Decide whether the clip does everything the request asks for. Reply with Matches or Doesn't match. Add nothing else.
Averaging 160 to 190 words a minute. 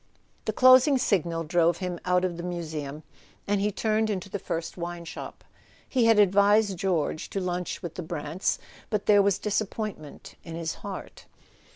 Matches